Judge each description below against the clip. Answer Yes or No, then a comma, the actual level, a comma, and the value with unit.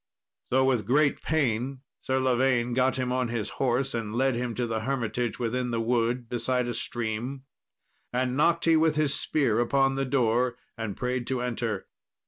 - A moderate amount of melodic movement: No, narrow, 2.1 semitones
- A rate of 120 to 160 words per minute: No, average, 175 wpm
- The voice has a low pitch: Yes, low, 125 Hz